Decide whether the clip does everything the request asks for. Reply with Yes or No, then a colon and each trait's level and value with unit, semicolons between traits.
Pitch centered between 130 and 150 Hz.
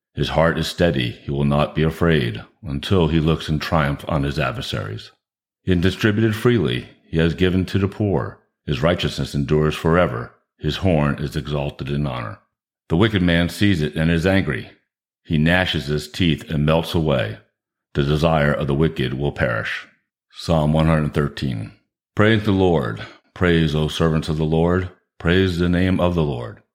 No: very low, 80 Hz